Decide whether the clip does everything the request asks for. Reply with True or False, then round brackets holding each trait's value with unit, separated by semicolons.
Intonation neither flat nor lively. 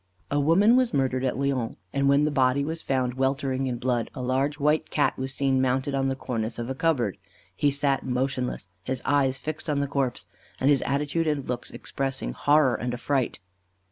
False (1.9 semitones)